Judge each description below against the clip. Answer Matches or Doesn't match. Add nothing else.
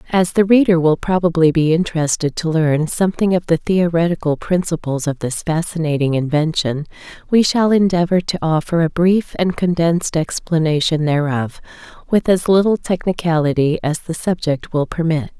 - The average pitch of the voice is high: Doesn't match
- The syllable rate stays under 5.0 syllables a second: Doesn't match